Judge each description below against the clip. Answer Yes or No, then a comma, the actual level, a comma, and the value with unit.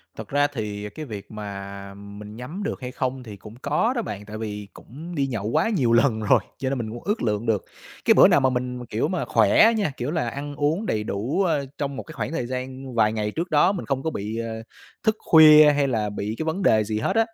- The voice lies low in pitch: Yes, low, 125 Hz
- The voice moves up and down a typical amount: No, wide, 5.9 semitones